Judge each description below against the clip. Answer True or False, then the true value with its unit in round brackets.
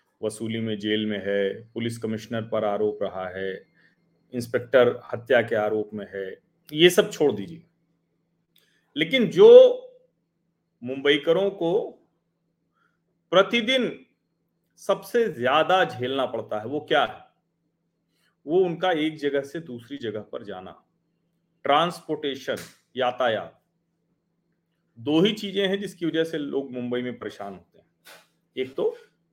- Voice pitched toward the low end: False (155 Hz)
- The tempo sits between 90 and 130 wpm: True (125 wpm)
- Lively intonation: True (7.5 semitones)